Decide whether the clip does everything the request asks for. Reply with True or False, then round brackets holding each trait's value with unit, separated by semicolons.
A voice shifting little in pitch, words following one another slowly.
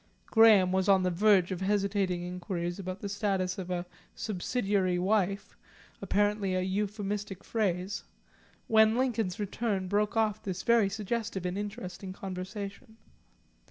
True (2.2 semitones; 130 wpm)